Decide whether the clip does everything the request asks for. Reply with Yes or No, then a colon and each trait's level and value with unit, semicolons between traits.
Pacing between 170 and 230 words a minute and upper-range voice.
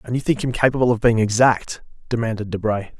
No: average, 200 wpm; low, 120 Hz